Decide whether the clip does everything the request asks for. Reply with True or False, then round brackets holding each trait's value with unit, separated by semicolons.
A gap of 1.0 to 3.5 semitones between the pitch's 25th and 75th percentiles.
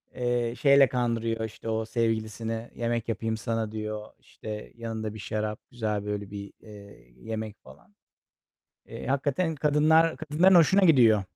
True (3.0 semitones)